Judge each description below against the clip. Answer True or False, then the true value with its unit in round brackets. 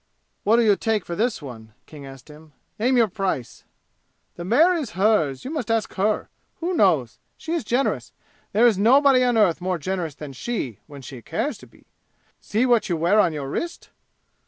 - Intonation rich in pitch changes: True (7.6 semitones)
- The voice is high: True (200 Hz)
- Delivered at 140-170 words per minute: False (190 wpm)